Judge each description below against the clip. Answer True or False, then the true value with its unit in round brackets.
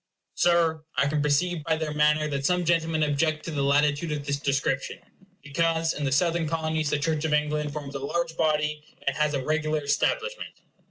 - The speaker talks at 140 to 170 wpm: False (195 wpm)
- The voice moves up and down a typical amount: False (2.0 semitones)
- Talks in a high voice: False (150 Hz)